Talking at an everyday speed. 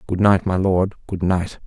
No: fast, 215 wpm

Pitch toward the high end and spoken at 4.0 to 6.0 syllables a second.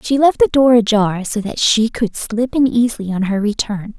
Yes: high, 225 Hz; 4.9 syllables/s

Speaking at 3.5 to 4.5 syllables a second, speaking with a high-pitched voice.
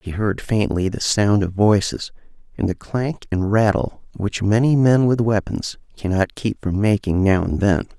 No: 4.4 syllables/s; low, 105 Hz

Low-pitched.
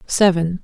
No: medium, 180 Hz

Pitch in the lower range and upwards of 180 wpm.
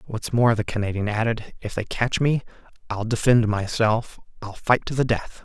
Yes: low, 110 Hz; average, 190 wpm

